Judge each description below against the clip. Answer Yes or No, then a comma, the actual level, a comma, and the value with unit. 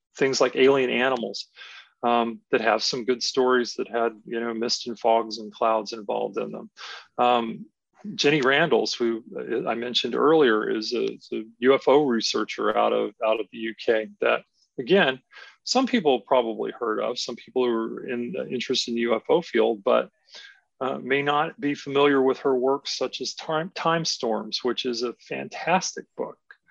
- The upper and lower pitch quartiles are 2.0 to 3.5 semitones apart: Yes, average, 2.8 semitones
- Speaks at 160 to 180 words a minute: Yes, average, 175 wpm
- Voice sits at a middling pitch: No, low, 120 Hz